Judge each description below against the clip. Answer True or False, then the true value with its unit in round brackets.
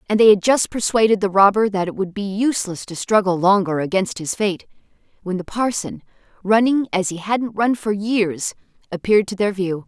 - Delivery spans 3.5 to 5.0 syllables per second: False (5.2 syllables/s)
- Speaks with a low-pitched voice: False (200 Hz)